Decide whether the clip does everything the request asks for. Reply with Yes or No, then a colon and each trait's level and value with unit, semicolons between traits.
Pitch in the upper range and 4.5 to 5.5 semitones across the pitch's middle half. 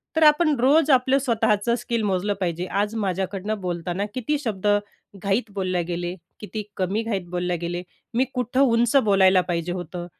Yes: high, 205 Hz; average, 4.8 semitones